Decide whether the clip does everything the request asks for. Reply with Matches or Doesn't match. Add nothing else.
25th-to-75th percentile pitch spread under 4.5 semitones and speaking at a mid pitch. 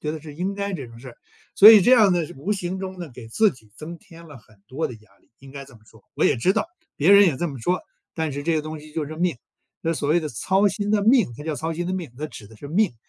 Doesn't match